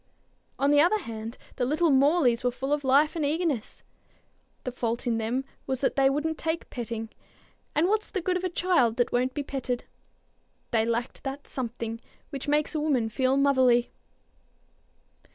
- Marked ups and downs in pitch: No, average, 4.0 semitones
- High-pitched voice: Yes, very high, 270 Hz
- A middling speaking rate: Yes, average, 170 wpm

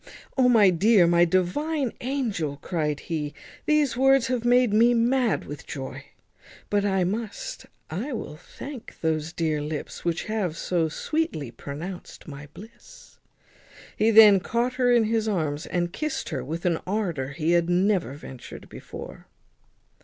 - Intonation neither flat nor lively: No, wide, 6.7 semitones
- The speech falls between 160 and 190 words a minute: No, average, 150 wpm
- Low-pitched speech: No, high, 190 Hz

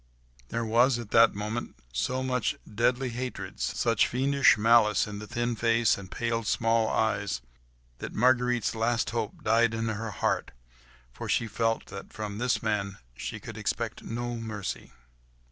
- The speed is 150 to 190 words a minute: Yes, average, 155 wpm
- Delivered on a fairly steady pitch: Yes, narrow, 2.0 semitones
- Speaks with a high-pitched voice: No, low, 115 Hz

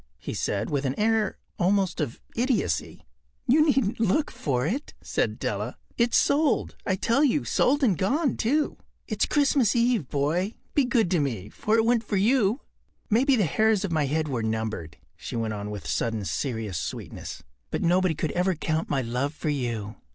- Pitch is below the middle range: No, medium, 185 Hz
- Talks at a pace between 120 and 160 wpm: No, average, 180 wpm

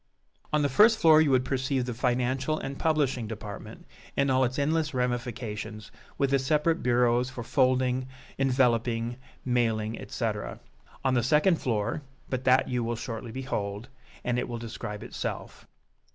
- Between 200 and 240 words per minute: No, average, 150 wpm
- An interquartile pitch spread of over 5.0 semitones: No, narrow, 2.4 semitones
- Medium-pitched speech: No, low, 125 Hz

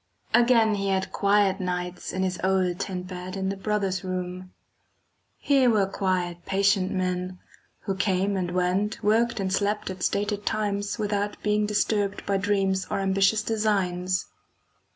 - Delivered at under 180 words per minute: Yes, average, 150 wpm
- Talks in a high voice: Yes, high, 195 Hz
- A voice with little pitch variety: Yes, narrow, 2.0 semitones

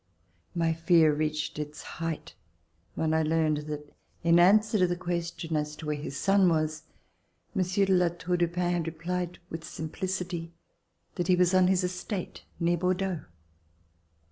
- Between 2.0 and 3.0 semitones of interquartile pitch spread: Yes, narrow, 2.4 semitones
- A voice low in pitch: No, medium, 170 Hz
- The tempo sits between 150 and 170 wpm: Yes, average, 160 wpm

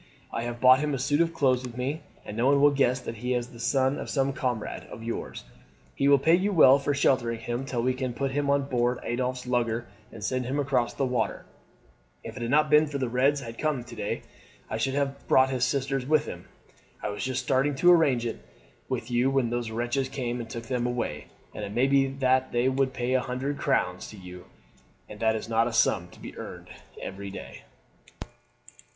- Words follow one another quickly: Yes, fast, 230 wpm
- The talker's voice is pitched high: No, low, 130 Hz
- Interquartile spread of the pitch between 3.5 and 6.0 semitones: No, narrow, 2.6 semitones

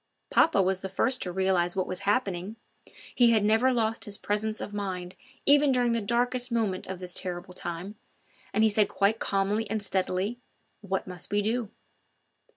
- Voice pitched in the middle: No, high, 205 Hz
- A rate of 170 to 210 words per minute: Yes, average, 180 wpm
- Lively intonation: No, average, 3.2 semitones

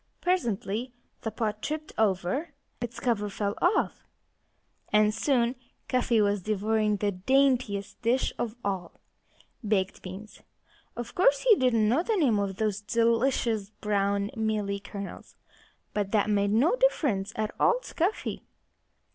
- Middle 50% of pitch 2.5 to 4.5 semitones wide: Yes, average, 3.8 semitones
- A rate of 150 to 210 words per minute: No, slow, 135 wpm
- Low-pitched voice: No, high, 215 Hz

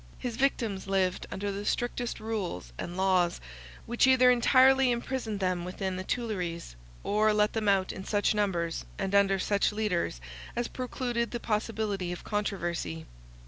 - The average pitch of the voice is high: Yes, high, 205 Hz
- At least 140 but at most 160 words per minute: Yes, average, 150 wpm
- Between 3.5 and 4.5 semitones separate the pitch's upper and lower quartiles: Yes, average, 4.1 semitones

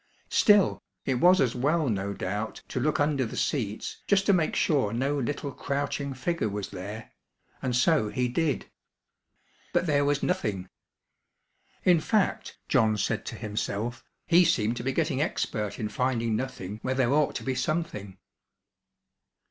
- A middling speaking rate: Yes, average, 155 wpm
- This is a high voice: No, low, 130 Hz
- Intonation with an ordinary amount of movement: No, wide, 5.7 semitones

